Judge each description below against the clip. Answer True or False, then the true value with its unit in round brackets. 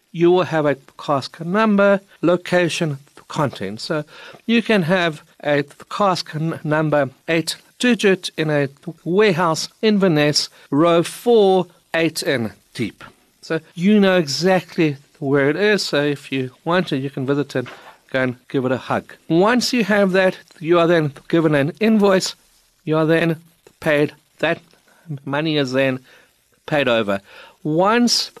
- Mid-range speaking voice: True (165 Hz)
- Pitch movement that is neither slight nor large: True (4.4 semitones)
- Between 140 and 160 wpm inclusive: True (145 wpm)